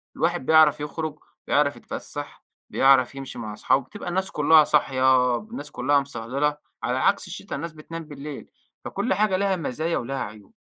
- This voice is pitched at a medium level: Yes, medium, 145 Hz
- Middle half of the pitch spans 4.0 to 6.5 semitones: No, average, 3.5 semitones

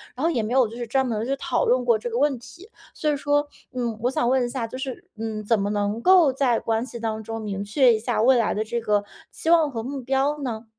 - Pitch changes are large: No, average, 3.3 semitones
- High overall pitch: Yes, high, 240 Hz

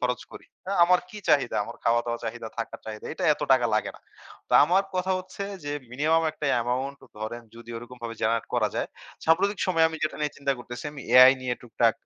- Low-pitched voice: Yes, low, 125 Hz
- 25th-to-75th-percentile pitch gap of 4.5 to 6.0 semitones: Yes, wide, 5.5 semitones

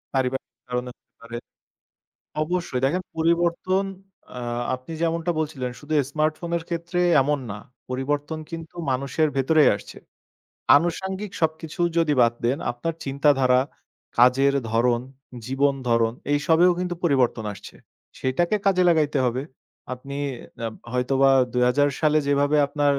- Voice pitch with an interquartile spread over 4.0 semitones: Yes, average, 4.4 semitones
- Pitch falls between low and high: Yes, medium, 145 Hz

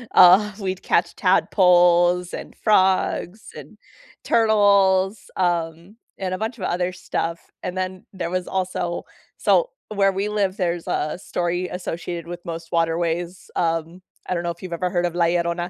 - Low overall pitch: No, medium, 180 Hz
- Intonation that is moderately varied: No, narrow, 1.8 semitones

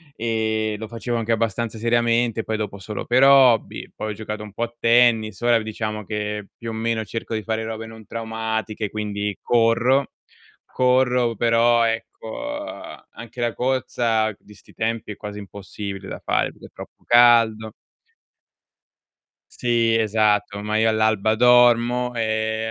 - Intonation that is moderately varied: No, narrow, 1.5 semitones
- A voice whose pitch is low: Yes, low, 110 Hz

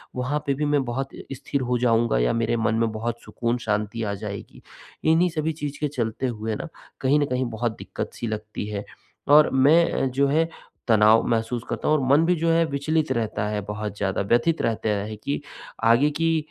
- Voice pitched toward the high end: No, low, 120 Hz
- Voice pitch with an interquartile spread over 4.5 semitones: Yes, average, 4.9 semitones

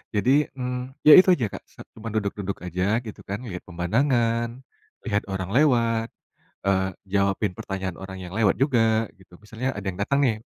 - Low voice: Yes, low, 105 Hz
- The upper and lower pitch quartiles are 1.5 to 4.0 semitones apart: No, average, 4.4 semitones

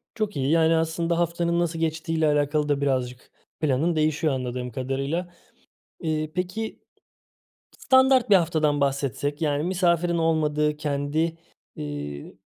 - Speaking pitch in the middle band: Yes, medium, 155 Hz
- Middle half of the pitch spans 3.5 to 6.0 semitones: No, average, 3.1 semitones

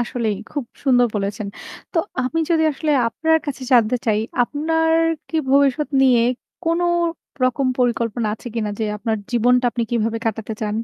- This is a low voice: No, high, 245 Hz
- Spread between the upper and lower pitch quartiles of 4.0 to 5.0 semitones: Yes, average, 4.3 semitones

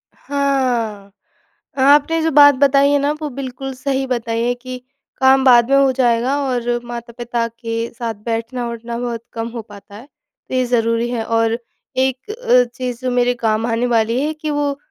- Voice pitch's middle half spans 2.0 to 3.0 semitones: Yes, narrow, 2.6 semitones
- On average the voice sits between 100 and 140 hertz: No, high, 245 Hz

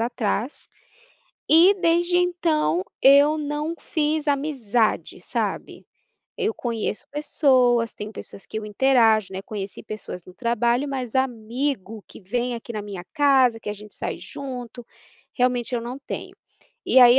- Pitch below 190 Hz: No, high, 245 Hz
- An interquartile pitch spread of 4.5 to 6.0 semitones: Yes, average, 4.8 semitones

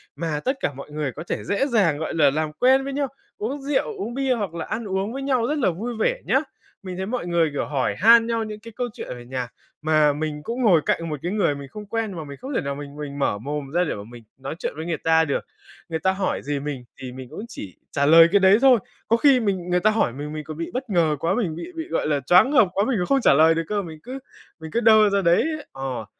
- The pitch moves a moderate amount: No, wide, 7.5 semitones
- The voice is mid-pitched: Yes, medium, 175 Hz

